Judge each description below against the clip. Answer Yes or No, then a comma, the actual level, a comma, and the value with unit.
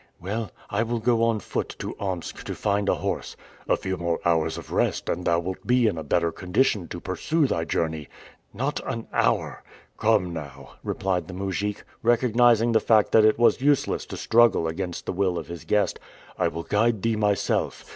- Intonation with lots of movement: No, average, 4.9 semitones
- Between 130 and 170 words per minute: No, average, 195 wpm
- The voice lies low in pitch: Yes, low, 100 Hz